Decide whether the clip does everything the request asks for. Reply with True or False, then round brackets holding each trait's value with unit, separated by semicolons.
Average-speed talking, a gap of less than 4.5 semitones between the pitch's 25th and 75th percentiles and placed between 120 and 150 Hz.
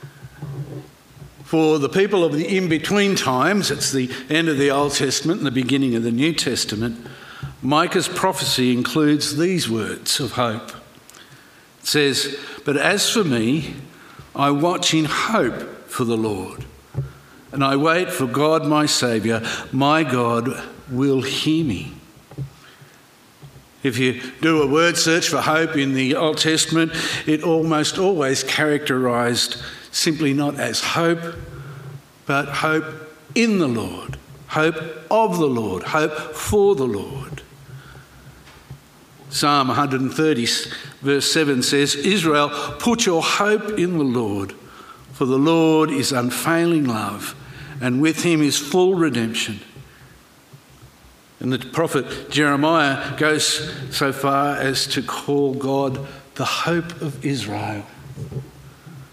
False (130 wpm; 2.9 semitones; 140 Hz)